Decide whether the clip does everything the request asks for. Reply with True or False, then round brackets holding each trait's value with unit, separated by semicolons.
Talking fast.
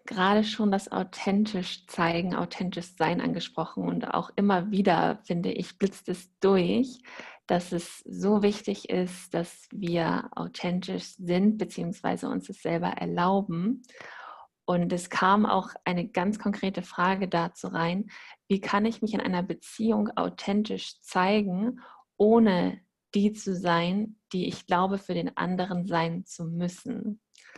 False (135 wpm)